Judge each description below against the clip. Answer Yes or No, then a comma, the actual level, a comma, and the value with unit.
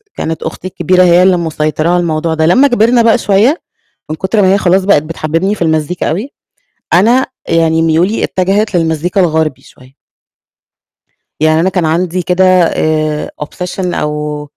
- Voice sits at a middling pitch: Yes, medium, 175 Hz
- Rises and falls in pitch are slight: No, average, 3.2 semitones